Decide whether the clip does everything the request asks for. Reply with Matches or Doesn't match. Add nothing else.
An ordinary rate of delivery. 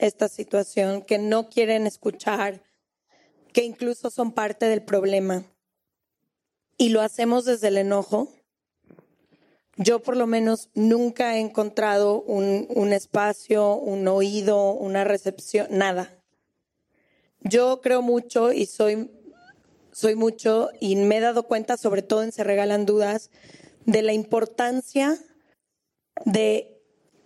Doesn't match